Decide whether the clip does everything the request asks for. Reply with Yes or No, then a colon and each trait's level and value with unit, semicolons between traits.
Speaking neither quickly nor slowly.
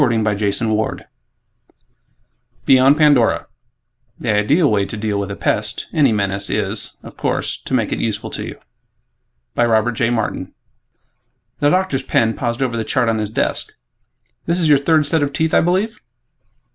Yes: average, 160 wpm